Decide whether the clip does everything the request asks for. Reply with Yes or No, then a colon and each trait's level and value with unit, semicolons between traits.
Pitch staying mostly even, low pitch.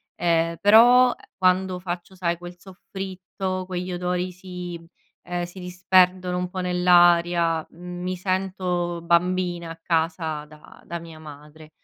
No: narrow, 1.3 semitones; medium, 180 Hz